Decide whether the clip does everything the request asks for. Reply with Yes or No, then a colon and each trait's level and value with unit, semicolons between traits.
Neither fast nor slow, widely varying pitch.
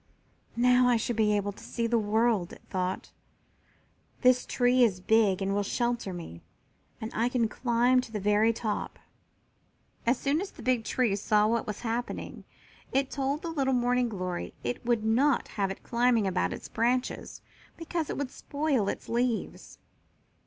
No: average, 170 wpm; average, 3.2 semitones